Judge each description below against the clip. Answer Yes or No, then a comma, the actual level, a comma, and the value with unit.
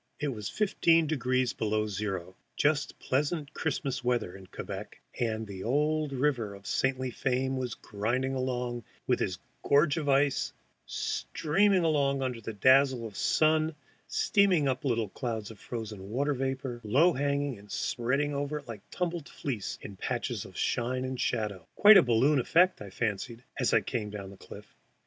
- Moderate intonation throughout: Yes, average, 4.5 semitones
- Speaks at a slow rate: No, average, 165 wpm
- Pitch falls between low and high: No, low, 130 Hz